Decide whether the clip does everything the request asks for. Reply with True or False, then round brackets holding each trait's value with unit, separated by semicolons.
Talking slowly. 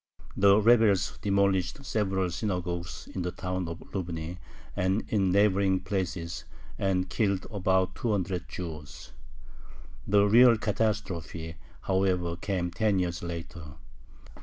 True (115 wpm)